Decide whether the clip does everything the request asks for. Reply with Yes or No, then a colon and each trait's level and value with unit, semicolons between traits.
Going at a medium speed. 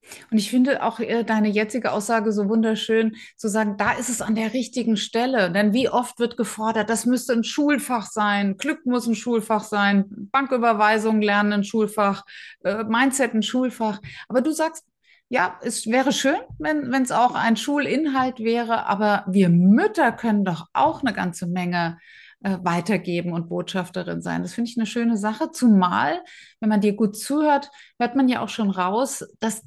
Yes: average, 175 wpm